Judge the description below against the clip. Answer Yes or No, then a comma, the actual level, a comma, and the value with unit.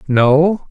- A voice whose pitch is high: No, medium, 150 Hz